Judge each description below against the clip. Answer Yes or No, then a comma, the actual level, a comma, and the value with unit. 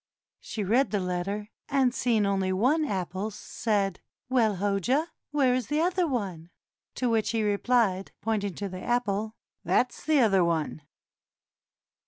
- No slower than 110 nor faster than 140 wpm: No, average, 150 wpm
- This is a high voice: Yes, high, 215 Hz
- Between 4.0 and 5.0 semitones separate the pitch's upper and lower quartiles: Yes, average, 4.3 semitones